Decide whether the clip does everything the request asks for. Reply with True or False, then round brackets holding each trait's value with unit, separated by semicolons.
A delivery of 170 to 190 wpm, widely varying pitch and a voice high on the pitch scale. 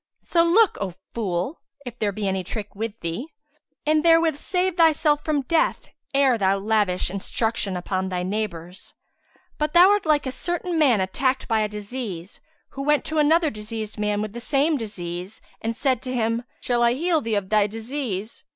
True (180 wpm; 6.7 semitones; 230 Hz)